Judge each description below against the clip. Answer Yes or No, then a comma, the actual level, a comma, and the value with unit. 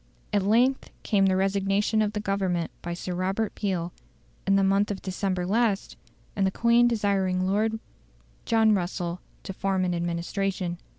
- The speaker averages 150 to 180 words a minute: Yes, average, 160 wpm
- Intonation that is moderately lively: No, narrow, 2.2 semitones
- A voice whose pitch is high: Yes, high, 195 Hz